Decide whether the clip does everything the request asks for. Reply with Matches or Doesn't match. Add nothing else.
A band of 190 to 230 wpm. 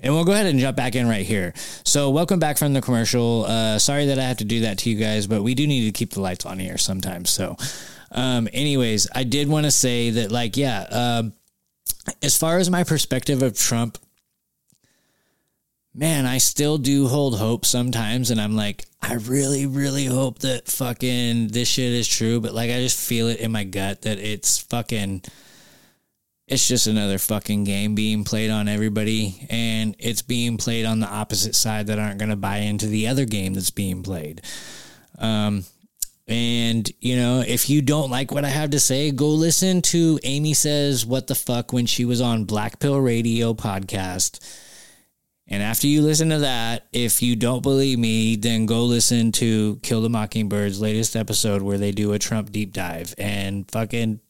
Matches